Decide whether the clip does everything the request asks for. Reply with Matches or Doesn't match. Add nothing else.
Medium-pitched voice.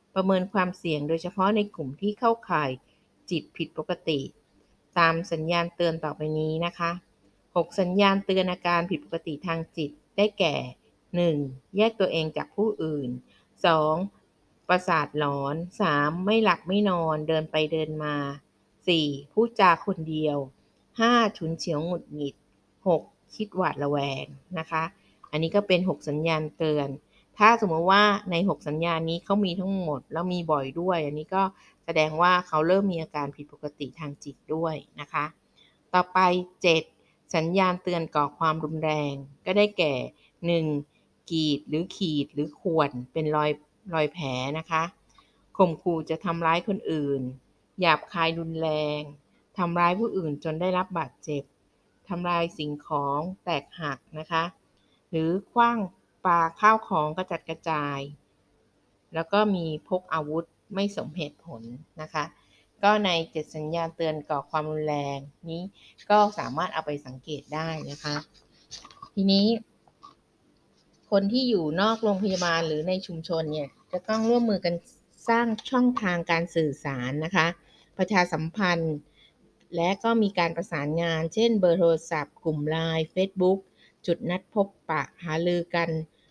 Matches